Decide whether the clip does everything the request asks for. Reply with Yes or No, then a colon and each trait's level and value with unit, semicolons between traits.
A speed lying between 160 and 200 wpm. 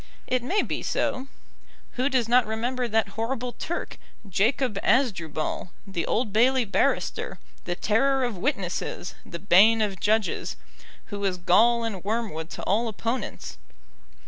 No: average, 140 wpm